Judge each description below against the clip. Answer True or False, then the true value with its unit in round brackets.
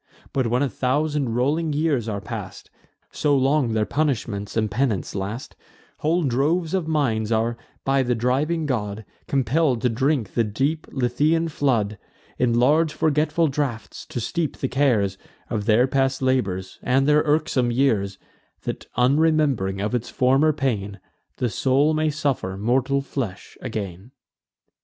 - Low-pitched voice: True (130 Hz)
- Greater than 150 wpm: False (145 wpm)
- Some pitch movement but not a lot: True (4.8 semitones)